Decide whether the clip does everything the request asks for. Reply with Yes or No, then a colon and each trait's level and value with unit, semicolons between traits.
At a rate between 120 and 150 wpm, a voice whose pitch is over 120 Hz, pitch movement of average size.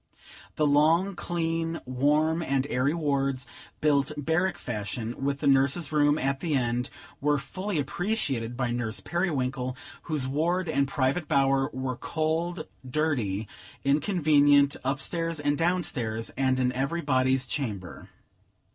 Yes: slow, 135 wpm; medium, 140 Hz; average, 3.6 semitones